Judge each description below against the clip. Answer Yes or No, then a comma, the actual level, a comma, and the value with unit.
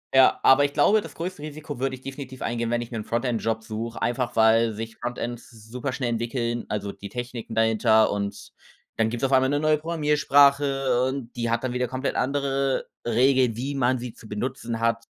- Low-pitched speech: Yes, low, 125 Hz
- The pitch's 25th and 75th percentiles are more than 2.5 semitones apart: Yes, average, 2.9 semitones